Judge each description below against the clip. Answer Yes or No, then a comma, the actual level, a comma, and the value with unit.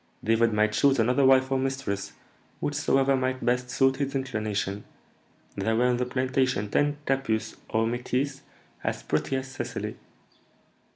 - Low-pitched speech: Yes, low, 130 Hz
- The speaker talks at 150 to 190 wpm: No, average, 140 wpm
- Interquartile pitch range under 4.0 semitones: Yes, average, 3.0 semitones